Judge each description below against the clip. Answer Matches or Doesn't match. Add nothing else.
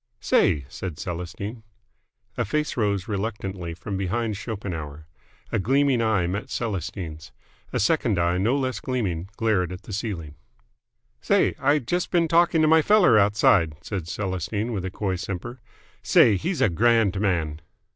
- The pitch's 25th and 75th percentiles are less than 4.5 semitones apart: Doesn't match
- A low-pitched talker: Matches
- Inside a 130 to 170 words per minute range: Matches